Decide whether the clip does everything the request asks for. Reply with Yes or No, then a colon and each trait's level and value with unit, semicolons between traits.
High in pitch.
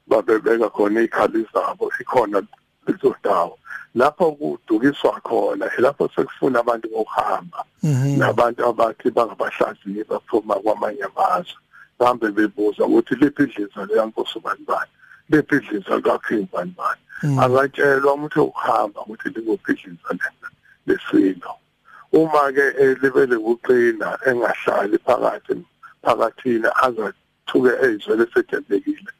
Yes: very high, 320 Hz